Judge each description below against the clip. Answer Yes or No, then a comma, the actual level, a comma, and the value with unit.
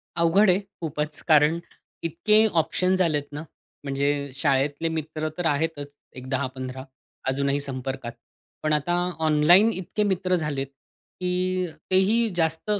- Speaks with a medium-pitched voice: Yes, medium, 155 Hz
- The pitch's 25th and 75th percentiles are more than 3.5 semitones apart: Yes, average, 4.2 semitones